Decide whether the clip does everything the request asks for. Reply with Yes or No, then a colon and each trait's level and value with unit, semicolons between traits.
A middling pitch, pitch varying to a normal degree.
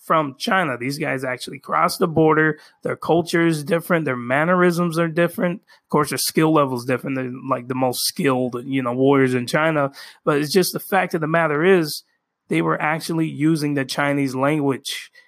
Yes: medium, 155 Hz; average, 4.1 semitones